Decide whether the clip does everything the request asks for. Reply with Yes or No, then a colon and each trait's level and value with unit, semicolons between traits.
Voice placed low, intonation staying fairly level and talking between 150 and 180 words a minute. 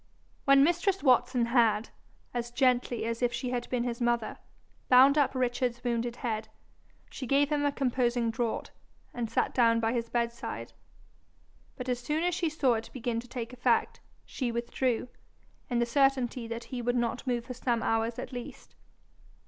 No: high, 245 Hz; narrow, 1.7 semitones; average, 175 wpm